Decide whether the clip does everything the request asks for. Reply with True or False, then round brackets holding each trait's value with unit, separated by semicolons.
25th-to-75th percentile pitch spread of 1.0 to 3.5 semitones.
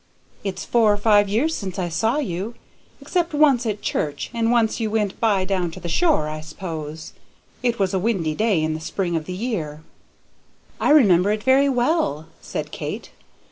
False (5.5 semitones)